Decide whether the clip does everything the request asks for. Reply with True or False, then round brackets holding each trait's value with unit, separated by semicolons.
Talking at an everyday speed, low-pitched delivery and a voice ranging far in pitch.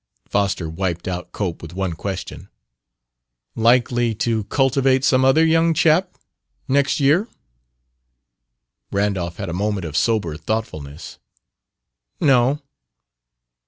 False (105 wpm; 110 Hz; 6.8 semitones)